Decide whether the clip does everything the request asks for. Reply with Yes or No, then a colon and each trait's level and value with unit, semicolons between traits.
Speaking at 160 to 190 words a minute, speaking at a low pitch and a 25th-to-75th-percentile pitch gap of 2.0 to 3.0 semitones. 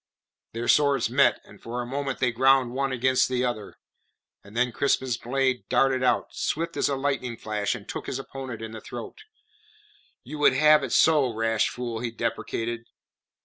Yes: average, 175 wpm; low, 125 Hz; narrow, 2.5 semitones